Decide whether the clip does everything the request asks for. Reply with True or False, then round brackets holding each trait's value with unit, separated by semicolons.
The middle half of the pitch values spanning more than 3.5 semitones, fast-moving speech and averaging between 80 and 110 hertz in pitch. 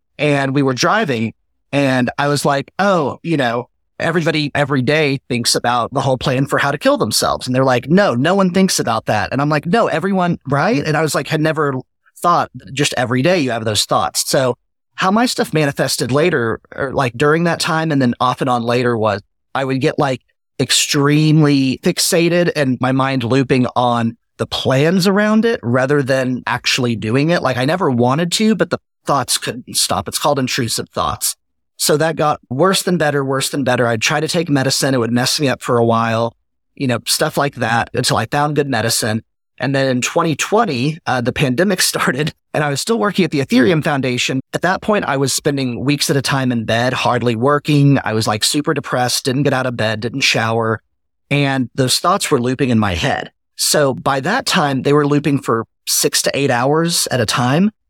False (4.0 semitones; 210 wpm; 140 Hz)